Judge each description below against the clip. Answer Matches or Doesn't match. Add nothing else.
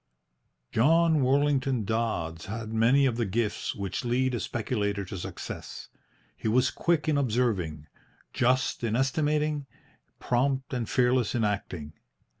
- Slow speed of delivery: Matches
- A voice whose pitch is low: Matches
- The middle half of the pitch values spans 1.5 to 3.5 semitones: Doesn't match